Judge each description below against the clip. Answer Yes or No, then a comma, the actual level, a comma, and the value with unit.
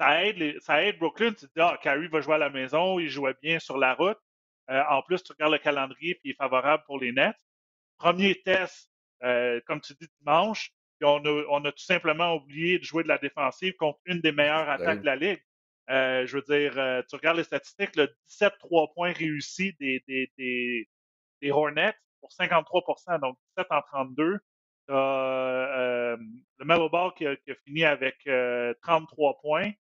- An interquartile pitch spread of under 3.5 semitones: No, average, 4.0 semitones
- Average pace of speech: Yes, average, 200 wpm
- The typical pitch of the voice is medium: Yes, medium, 150 Hz